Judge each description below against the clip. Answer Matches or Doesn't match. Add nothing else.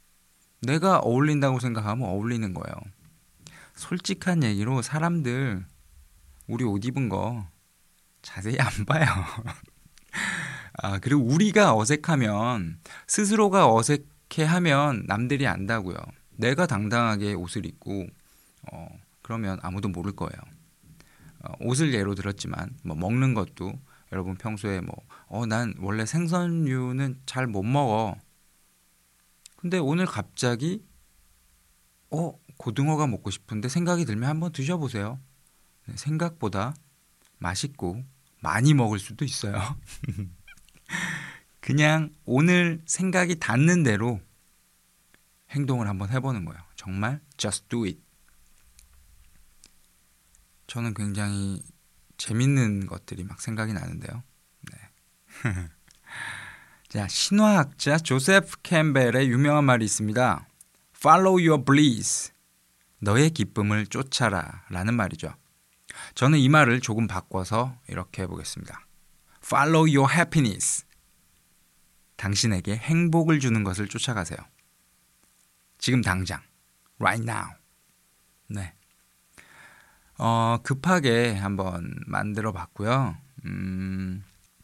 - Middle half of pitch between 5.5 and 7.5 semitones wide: Matches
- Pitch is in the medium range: Doesn't match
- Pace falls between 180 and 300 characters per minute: Matches